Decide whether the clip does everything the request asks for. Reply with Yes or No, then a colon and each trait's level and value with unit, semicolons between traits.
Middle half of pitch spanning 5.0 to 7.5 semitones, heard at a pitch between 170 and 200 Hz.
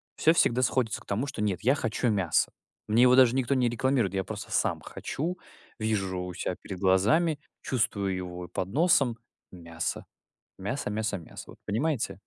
No: wide, 5.4 semitones; low, 110 Hz